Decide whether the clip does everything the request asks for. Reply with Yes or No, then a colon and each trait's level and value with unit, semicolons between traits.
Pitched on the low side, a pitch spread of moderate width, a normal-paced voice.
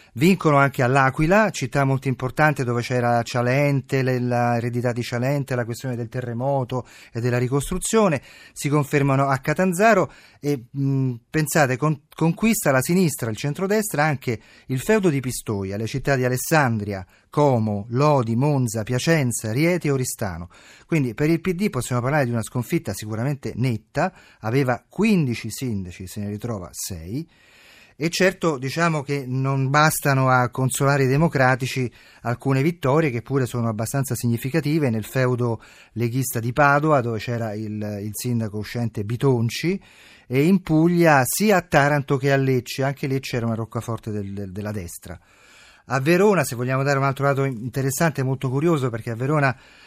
Yes: low, 130 Hz; average, 3.9 semitones; average, 155 wpm